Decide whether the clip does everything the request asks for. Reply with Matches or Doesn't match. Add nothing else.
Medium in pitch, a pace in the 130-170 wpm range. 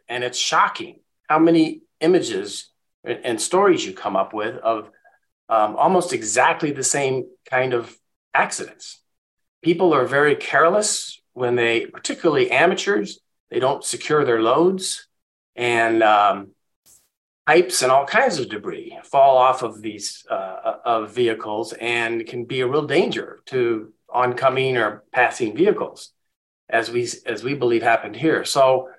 Matches